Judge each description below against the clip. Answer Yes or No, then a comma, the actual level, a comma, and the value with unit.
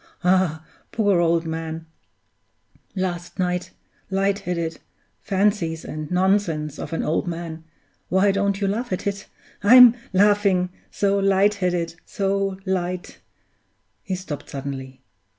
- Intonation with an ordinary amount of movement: Yes, average, 3.2 semitones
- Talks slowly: Yes, slow, 125 wpm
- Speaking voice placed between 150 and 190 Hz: Yes, medium, 185 Hz